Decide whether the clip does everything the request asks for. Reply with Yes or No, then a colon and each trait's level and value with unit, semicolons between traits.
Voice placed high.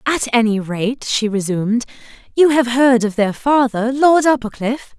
Yes: high, 240 Hz